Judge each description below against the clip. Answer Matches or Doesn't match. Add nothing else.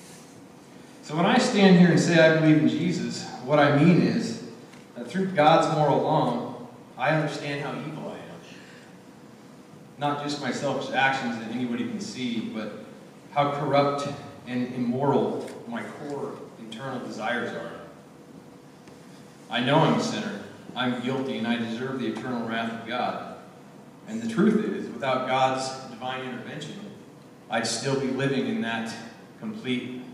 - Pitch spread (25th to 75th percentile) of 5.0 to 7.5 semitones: Matches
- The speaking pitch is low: Doesn't match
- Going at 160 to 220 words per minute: Doesn't match